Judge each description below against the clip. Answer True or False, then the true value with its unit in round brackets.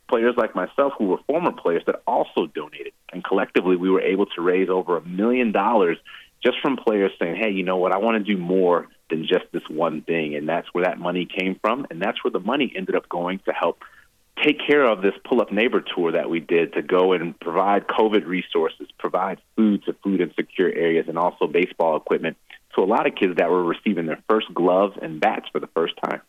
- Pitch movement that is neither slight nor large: True (3.5 semitones)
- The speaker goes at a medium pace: False (230 wpm)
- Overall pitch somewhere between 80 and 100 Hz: True (95 Hz)